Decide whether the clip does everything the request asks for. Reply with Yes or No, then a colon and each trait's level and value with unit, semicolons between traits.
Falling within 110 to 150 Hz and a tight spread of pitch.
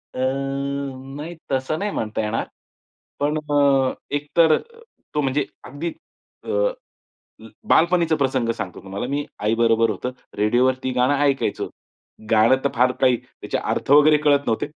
No: low, 135 Hz; average, 3.1 semitones